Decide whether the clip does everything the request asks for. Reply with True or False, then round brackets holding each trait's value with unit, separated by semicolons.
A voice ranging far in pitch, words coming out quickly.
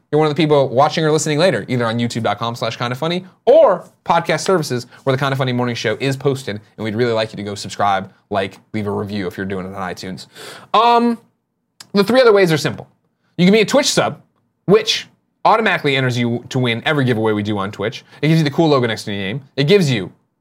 True (6.3 semitones; 245 wpm)